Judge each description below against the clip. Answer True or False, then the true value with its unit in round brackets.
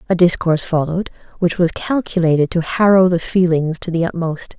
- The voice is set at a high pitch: False (170 Hz)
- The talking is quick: False (170 wpm)